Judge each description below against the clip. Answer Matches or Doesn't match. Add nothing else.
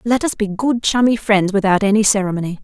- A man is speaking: Doesn't match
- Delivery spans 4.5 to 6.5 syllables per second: Matches